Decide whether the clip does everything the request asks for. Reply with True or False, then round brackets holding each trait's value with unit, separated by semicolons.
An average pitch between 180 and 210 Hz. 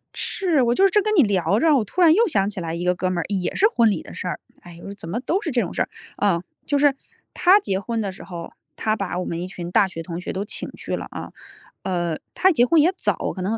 True (200 Hz)